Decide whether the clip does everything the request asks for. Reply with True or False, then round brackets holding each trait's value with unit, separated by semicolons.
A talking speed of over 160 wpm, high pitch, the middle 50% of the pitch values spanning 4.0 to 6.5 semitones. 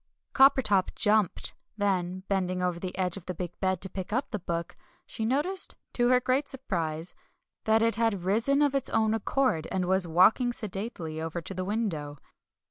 True (180 wpm; 195 Hz; 4.4 semitones)